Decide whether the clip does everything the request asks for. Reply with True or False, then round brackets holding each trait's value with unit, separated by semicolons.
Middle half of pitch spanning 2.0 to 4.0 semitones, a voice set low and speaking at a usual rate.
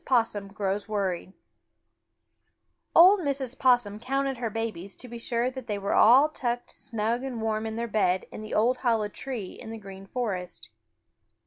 False (3.6 semitones; 225 Hz; 165 wpm)